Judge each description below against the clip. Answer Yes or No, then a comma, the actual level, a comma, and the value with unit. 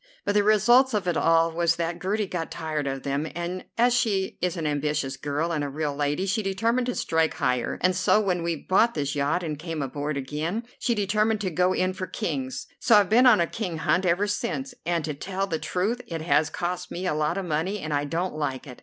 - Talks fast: Yes, fast, 235 wpm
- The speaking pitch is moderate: Yes, medium, 175 Hz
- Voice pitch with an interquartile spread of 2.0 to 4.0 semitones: No, average, 4.7 semitones